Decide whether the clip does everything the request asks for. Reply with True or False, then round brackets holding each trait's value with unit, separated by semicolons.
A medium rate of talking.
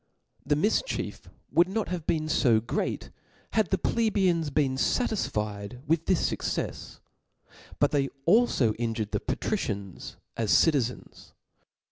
False (120 wpm)